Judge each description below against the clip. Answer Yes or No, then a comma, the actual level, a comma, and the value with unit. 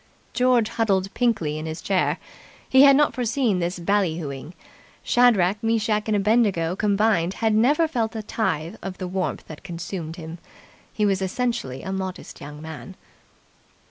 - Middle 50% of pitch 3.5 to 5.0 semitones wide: Yes, average, 4.7 semitones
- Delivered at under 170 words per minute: Yes, average, 155 wpm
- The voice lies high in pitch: Yes, high, 195 Hz